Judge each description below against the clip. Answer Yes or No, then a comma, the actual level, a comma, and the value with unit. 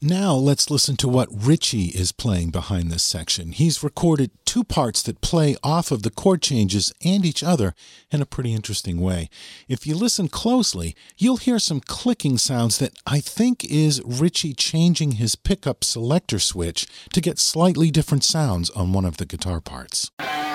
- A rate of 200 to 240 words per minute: No, average, 175 wpm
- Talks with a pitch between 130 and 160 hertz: Yes, medium, 140 Hz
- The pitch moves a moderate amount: No, wide, 8.9 semitones